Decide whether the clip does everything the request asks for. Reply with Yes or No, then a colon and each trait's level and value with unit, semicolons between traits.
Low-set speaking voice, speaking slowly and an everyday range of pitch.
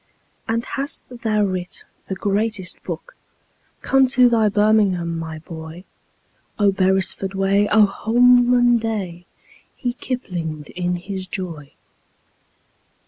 No: high, 200 Hz; slow, 110 wpm; average, 4.2 semitones